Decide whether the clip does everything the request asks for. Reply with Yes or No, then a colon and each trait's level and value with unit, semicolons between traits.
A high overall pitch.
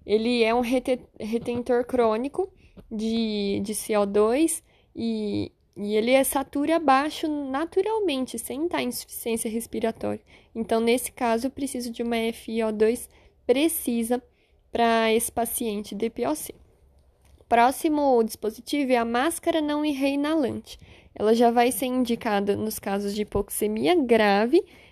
Yes: high, 235 Hz